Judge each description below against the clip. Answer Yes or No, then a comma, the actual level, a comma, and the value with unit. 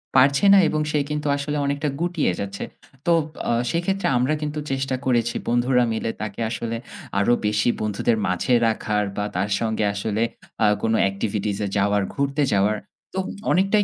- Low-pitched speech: Yes, low, 120 Hz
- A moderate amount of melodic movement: No, wide, 5.9 semitones